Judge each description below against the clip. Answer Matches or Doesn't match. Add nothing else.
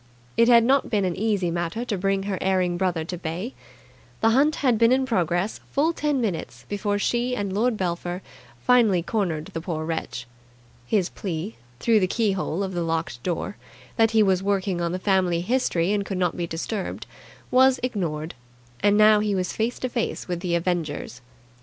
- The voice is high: Matches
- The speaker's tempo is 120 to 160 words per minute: Doesn't match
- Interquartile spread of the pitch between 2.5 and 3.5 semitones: Doesn't match